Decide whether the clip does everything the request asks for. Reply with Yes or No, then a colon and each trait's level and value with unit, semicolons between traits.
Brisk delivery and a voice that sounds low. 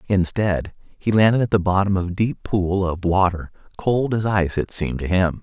Yes: fast, 210 wpm; very low, 95 Hz